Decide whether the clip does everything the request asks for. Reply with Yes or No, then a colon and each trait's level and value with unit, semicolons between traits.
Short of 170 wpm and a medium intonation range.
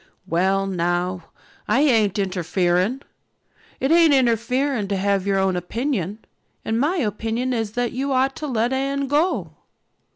No: average, 140 wpm; wide, 5.7 semitones